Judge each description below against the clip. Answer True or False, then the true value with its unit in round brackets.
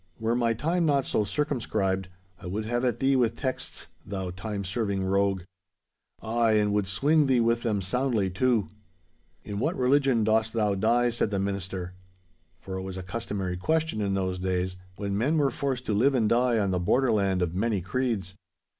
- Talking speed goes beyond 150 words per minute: True (185 wpm)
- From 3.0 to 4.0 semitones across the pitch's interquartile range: False (4.4 semitones)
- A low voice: True (110 Hz)